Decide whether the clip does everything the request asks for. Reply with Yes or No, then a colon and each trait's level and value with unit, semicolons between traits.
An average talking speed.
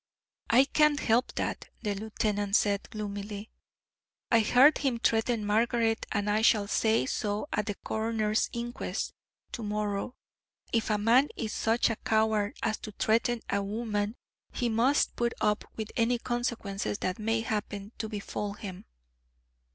Yes: average, 150 wpm